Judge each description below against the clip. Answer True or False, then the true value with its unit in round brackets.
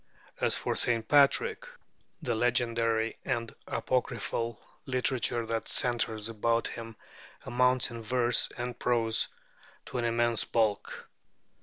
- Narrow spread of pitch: True (1.4 semitones)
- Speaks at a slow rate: True (115 wpm)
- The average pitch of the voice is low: True (120 Hz)